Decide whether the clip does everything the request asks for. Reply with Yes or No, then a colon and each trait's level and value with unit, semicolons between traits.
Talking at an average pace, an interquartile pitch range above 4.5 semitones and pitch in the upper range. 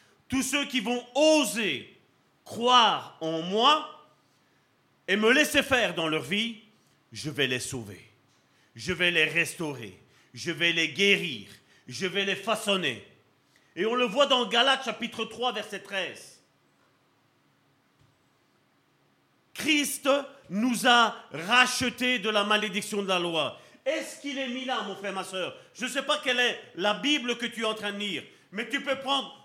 Yes: average, 160 wpm; average, 5.2 semitones; high, 225 Hz